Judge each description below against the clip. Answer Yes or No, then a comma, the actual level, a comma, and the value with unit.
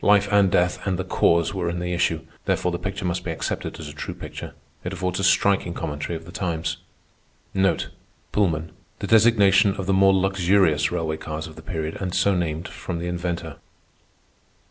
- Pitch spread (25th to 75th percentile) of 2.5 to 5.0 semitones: Yes, average, 2.8 semitones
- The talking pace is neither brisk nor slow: Yes, average, 185 wpm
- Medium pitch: No, very low, 90 Hz